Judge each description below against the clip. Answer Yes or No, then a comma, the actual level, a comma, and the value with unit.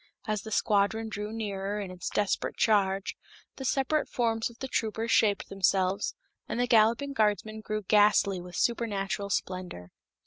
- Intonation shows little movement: Yes, narrow, 2.3 semitones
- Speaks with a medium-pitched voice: No, high, 210 Hz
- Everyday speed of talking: Yes, average, 150 wpm